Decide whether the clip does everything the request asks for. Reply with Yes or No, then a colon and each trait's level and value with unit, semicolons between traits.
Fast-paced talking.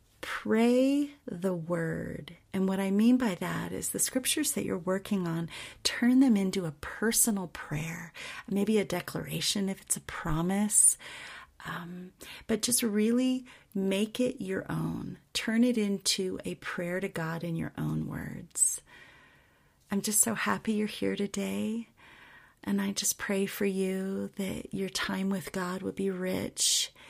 No: average, 155 wpm